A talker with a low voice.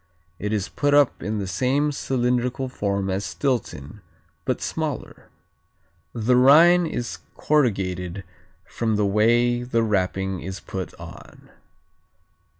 Yes: low, 115 Hz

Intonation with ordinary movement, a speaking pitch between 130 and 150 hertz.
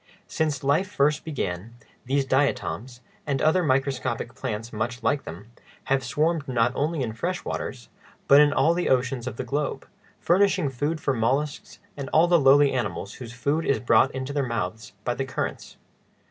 Yes: average, 3.7 semitones; low, 135 Hz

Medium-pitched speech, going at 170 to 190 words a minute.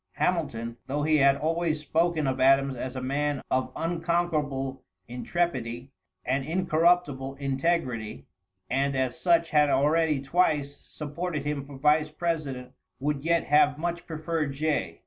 No: medium, 145 Hz; slow, 135 wpm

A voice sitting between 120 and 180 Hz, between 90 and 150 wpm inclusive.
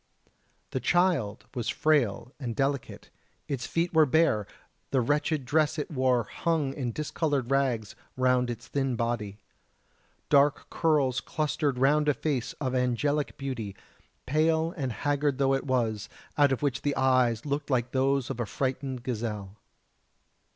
Yes: low, 135 Hz; average, 145 wpm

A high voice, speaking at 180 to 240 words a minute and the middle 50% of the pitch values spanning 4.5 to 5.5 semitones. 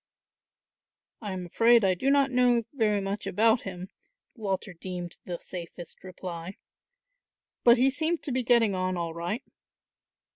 No: high, 200 Hz; average, 145 wpm; average, 5.0 semitones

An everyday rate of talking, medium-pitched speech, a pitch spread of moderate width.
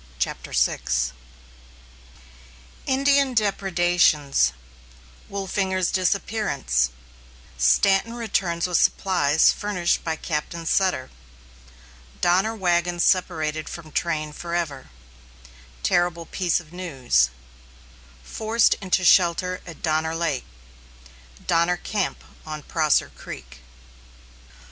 No: slow, 85 wpm; medium, 175 Hz; average, 3.7 semitones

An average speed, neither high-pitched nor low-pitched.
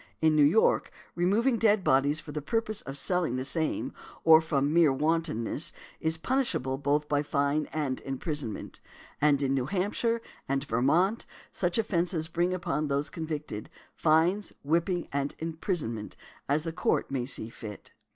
Yes: average, 150 wpm; medium, 155 Hz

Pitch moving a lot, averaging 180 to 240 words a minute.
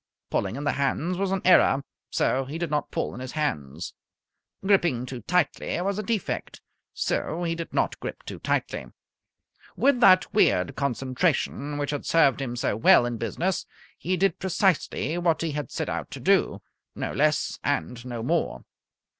No: wide, 5.9 semitones; average, 170 wpm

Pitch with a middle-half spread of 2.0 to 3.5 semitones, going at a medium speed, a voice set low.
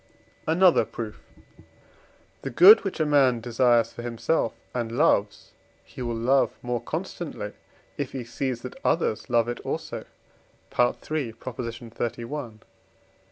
No: average, 2.7 semitones; slow, 120 wpm; low, 120 Hz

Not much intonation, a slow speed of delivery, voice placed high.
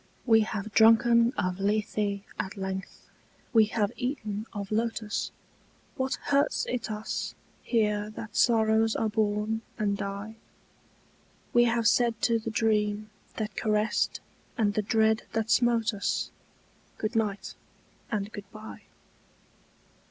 Yes: narrow, 1.5 semitones; slow, 120 wpm; high, 215 Hz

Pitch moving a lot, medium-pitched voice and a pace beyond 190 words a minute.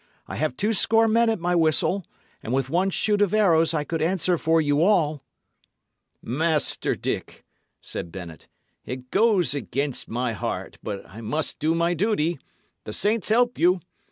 No: wide, 5.7 semitones; medium, 165 Hz; average, 165 wpm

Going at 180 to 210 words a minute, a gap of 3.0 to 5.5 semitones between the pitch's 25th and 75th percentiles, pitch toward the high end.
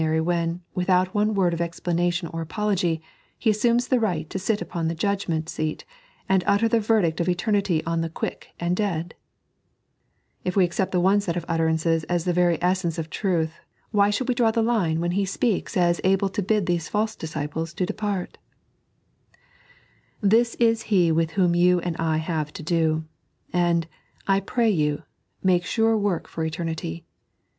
No: average, 185 wpm; average, 3.6 semitones; medium, 175 Hz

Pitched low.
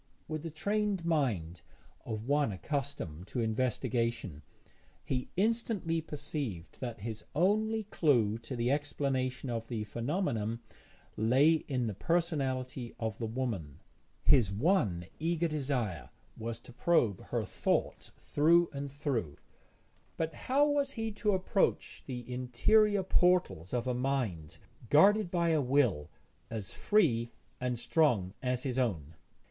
Yes: low, 130 Hz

